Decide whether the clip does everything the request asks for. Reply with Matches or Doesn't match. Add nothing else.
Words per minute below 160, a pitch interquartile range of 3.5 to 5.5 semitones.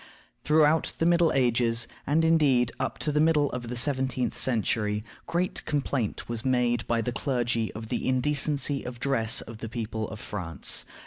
Doesn't match